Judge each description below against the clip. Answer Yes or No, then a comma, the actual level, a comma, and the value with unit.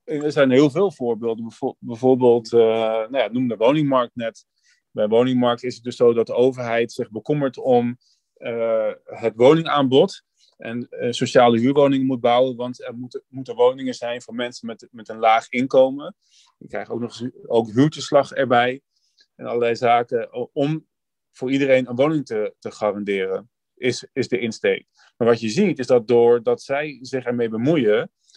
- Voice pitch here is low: Yes, low, 125 Hz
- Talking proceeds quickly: No, average, 170 wpm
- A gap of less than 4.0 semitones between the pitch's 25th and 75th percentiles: Yes, average, 2.7 semitones